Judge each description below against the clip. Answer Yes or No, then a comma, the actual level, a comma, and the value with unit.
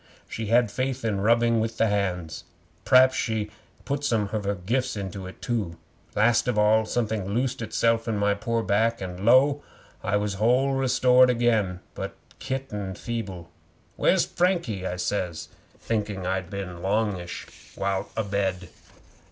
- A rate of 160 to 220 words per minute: No, average, 150 wpm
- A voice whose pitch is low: Yes, low, 105 Hz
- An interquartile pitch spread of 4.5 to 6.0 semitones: No, average, 3.5 semitones